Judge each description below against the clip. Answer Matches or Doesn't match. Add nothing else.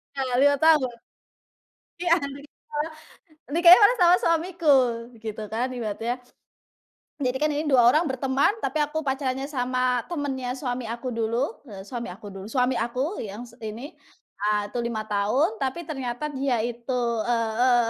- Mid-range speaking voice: Doesn't match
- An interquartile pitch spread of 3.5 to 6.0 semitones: Matches